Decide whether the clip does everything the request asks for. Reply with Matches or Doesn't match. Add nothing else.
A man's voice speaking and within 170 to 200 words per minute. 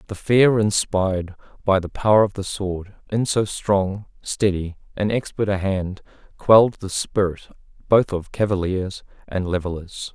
Doesn't match